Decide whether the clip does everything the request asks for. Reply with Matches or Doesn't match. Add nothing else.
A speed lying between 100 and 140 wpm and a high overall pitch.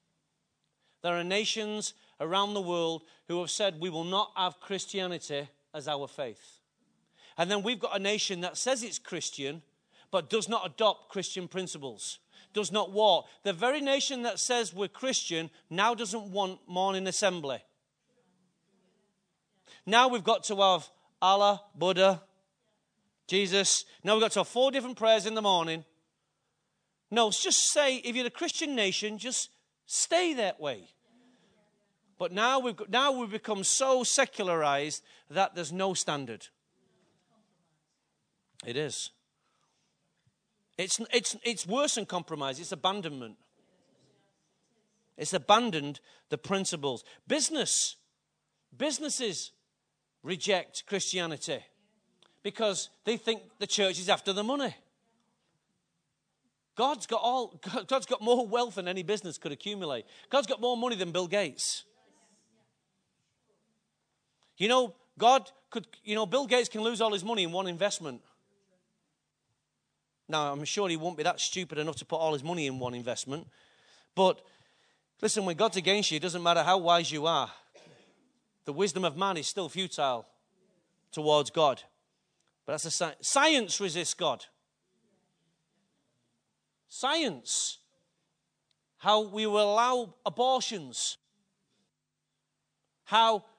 Matches